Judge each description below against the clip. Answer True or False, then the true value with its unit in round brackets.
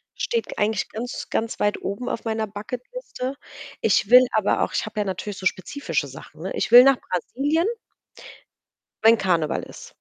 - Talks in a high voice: True (220 Hz)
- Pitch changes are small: False (4.3 semitones)